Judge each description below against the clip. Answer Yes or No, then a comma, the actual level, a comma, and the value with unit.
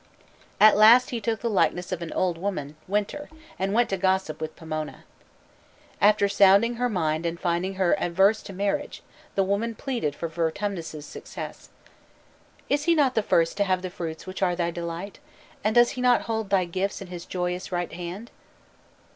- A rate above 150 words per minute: Yes, average, 180 wpm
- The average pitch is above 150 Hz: Yes, high, 190 Hz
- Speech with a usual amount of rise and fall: Yes, average, 3.8 semitones